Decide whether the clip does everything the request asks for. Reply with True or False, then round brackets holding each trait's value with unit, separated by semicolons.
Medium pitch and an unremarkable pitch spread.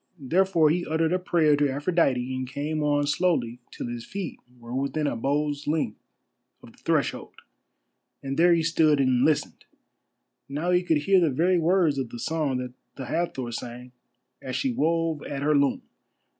True (150 Hz; 3.9 semitones)